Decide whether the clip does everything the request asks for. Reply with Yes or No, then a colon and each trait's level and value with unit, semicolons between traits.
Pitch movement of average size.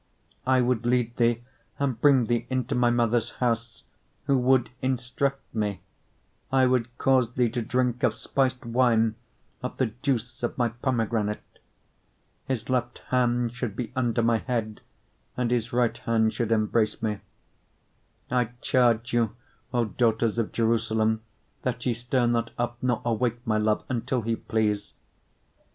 No: narrow, 1.8 semitones